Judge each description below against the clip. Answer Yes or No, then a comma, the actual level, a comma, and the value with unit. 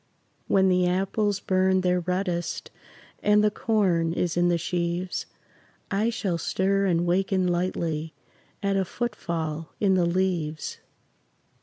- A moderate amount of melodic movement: No, narrow, 2.2 semitones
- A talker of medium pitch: Yes, medium, 180 Hz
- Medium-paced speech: No, slow, 130 wpm